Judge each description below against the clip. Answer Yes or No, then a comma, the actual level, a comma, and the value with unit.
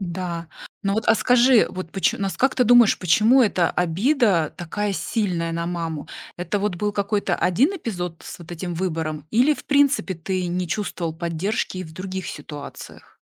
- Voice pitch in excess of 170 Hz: Yes, medium, 185 Hz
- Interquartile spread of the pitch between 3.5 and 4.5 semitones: Yes, average, 4.2 semitones